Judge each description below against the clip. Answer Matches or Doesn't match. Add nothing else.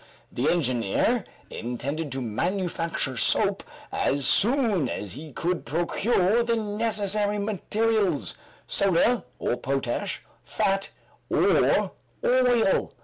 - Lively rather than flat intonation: Matches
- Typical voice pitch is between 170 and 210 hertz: Matches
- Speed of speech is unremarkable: Doesn't match